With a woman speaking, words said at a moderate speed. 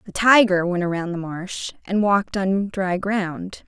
Yes: female; average, 180 wpm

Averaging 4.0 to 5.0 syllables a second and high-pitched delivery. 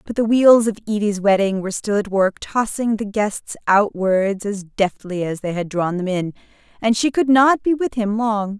Yes: 4.6 syllables/s; high, 210 Hz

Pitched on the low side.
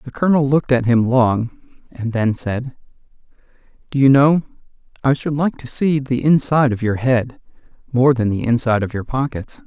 Yes: low, 125 Hz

